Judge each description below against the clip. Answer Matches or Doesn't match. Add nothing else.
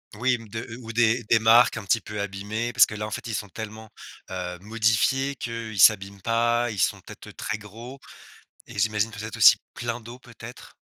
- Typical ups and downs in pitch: Doesn't match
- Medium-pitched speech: Doesn't match